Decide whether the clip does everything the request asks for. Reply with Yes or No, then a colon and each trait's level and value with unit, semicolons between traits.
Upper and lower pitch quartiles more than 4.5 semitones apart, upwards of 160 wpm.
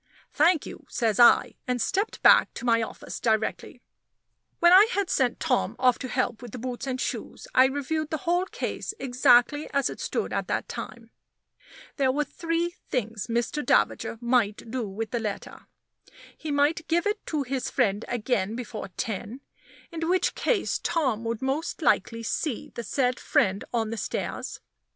Yes: average, 5.3 semitones; average, 170 wpm